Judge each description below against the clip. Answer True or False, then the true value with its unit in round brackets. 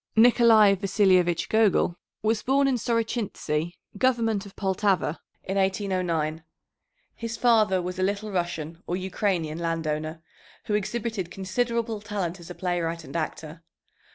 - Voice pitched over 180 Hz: True (190 Hz)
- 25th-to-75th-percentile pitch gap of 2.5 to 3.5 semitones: False (4.3 semitones)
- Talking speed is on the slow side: True (125 wpm)